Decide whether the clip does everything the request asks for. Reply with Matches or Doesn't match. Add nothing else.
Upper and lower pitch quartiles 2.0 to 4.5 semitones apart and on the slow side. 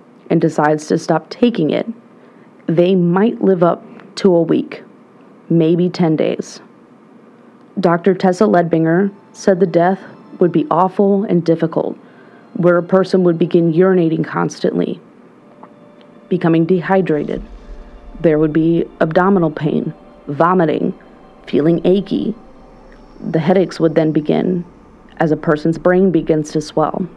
Matches